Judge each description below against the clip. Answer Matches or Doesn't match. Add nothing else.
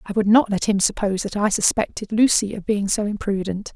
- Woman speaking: Matches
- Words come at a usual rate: Doesn't match